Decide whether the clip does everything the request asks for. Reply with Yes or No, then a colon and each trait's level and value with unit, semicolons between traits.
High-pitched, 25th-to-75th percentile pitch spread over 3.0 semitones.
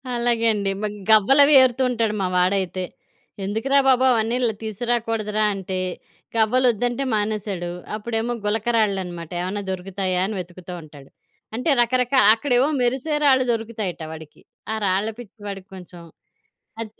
Yes: high, 215 Hz; average, 4.1 semitones